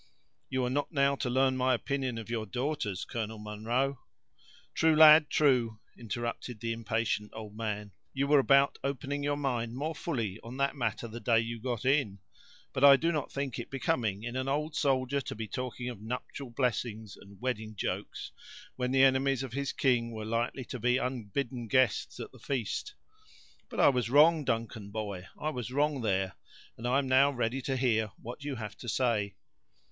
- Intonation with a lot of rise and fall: No, average, 3.4 semitones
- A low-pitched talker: Yes, low, 125 Hz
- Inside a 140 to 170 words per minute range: No, average, 190 wpm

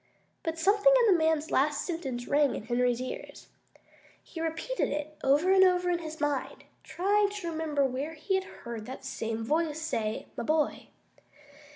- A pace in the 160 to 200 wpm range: Yes, average, 170 wpm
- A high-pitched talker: Yes, very high, 310 Hz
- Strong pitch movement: No, average, 4.4 semitones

